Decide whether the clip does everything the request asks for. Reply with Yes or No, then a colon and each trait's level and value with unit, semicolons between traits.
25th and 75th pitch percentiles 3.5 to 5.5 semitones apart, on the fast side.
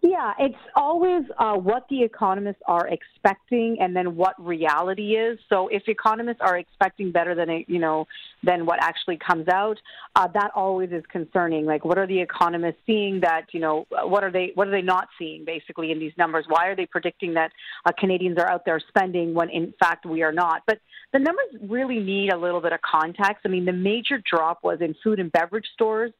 Yes: average, 3.9 semitones; fast, 210 wpm